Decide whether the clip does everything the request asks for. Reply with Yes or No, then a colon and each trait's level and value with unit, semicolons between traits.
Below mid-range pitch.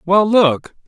No: high, 190 Hz